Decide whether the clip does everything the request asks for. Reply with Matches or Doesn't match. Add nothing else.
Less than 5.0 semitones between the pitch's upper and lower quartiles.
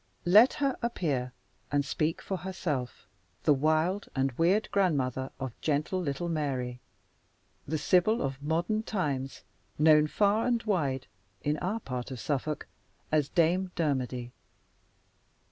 Doesn't match